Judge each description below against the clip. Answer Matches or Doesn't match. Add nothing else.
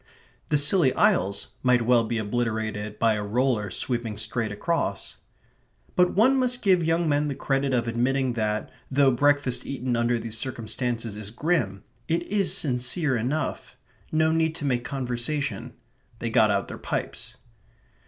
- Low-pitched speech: Matches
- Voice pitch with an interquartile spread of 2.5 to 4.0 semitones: Doesn't match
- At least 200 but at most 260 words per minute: Doesn't match